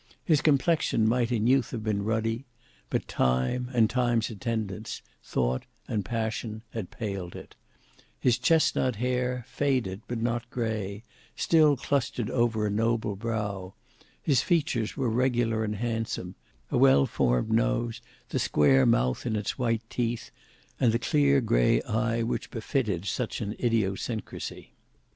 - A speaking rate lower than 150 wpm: Yes, average, 140 wpm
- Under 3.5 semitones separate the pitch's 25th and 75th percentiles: Yes, average, 2.8 semitones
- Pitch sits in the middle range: No, low, 115 Hz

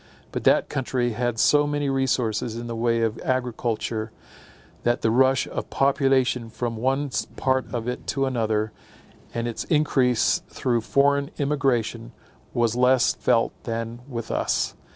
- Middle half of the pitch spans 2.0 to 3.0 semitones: Yes, narrow, 2.6 semitones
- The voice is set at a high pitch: No, low, 125 Hz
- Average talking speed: Yes, average, 145 wpm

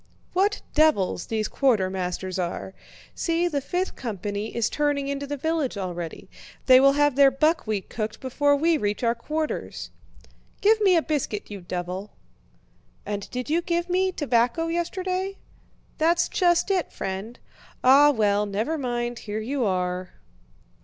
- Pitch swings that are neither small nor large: No, wide, 7.7 semitones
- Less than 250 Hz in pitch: No, very high, 265 Hz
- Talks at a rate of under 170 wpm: Yes, average, 145 wpm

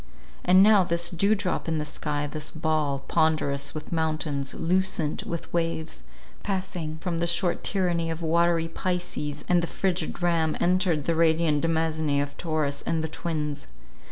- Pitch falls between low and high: Yes, medium, 165 Hz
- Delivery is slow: No, average, 155 wpm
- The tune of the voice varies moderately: No, narrow, 2.1 semitones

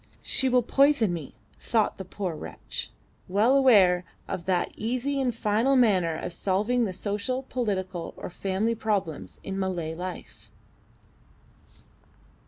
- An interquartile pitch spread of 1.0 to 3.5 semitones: No, average, 5.0 semitones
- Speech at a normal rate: No, slow, 130 wpm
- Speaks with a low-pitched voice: No, high, 205 Hz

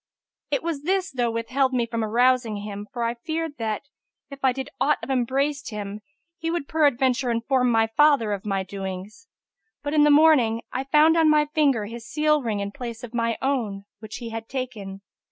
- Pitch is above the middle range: Yes, high, 245 Hz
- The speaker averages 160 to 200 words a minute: Yes, average, 195 wpm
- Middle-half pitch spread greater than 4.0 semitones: Yes, average, 4.5 semitones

